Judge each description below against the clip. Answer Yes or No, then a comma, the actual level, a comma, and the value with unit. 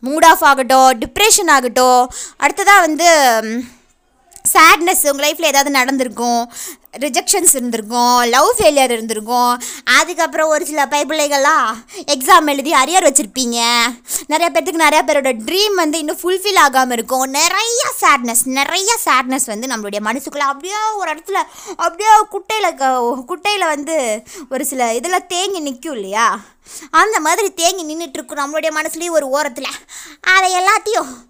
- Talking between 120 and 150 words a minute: Yes, average, 125 wpm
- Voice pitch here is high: Yes, very high, 300 Hz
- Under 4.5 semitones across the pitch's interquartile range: No, average, 5.2 semitones